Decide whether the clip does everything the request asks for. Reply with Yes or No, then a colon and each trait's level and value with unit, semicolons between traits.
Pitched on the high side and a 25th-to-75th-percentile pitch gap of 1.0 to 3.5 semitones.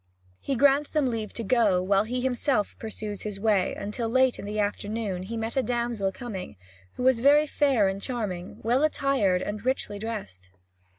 No: high, 225 Hz; average, 4.0 semitones